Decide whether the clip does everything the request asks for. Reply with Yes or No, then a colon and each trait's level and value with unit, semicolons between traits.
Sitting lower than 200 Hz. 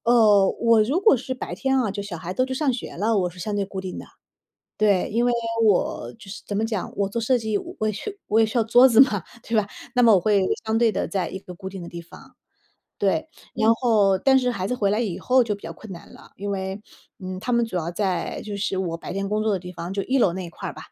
No: high, 210 Hz